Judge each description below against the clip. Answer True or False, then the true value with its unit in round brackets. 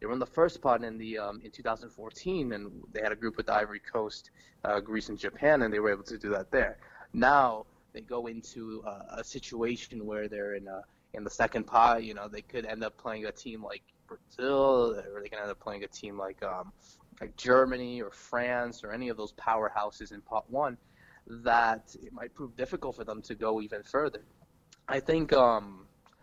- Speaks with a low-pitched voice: True (115 Hz)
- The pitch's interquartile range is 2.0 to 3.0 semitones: True (2.4 semitones)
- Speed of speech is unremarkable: False (215 wpm)